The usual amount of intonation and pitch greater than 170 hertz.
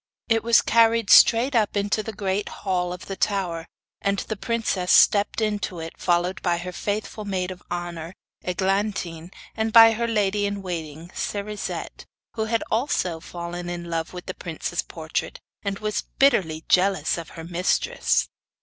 Yes: average, 3.4 semitones; high, 190 Hz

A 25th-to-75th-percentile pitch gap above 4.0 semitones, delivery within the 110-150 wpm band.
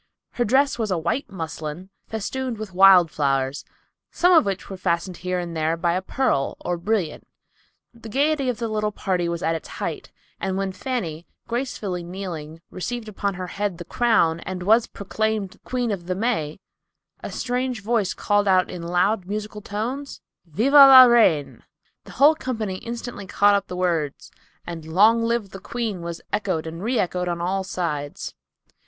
No: average, 5.0 semitones; average, 175 wpm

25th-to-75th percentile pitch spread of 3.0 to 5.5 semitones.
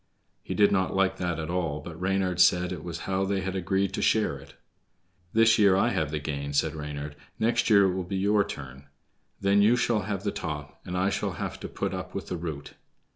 Yes: average, 4.1 semitones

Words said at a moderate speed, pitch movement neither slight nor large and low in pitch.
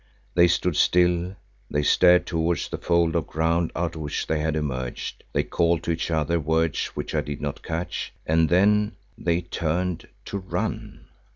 No: average, 170 wpm; narrow, 2.1 semitones; very low, 85 Hz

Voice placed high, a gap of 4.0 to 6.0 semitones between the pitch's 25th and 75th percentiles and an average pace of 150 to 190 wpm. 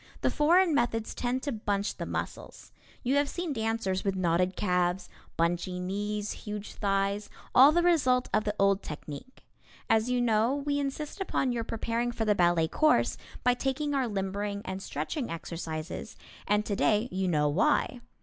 Yes: high, 210 Hz; average, 5.2 semitones; average, 165 wpm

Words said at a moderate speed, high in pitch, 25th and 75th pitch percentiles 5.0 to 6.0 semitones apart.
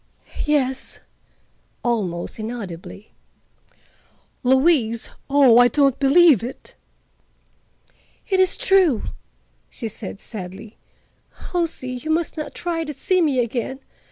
No: slow, 100 wpm; very high, 260 Hz; wide, 5.6 semitones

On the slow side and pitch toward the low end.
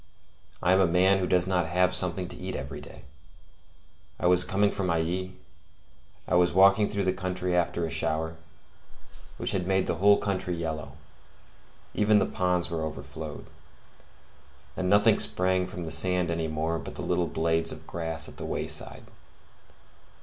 No: average, 165 wpm; very low, 90 Hz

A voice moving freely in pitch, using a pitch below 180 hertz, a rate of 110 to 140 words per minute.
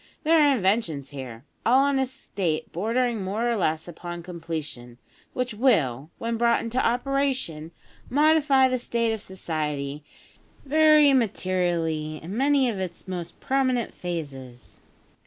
No: wide, 8.1 semitones; high, 200 Hz; slow, 135 wpm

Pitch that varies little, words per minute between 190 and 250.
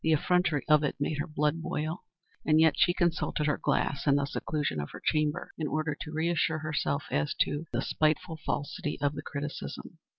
Yes: narrow, 1.7 semitones; average, 195 wpm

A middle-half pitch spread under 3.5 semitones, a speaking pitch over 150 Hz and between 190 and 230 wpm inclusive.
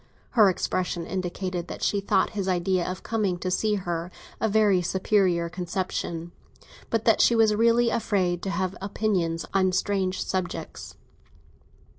No: average, 2.8 semitones; medium, 185 Hz; average, 145 wpm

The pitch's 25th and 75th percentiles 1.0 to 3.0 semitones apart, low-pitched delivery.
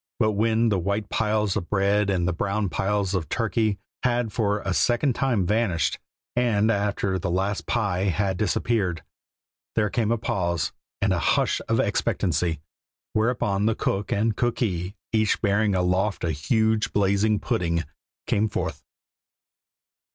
Yes: narrow, 2.6 semitones; low, 100 Hz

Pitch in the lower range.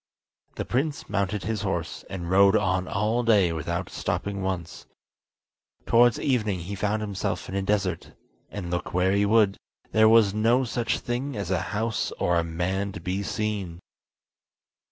Yes: low, 100 Hz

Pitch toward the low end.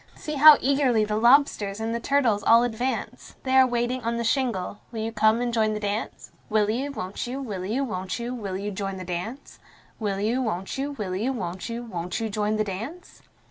No: high, 225 Hz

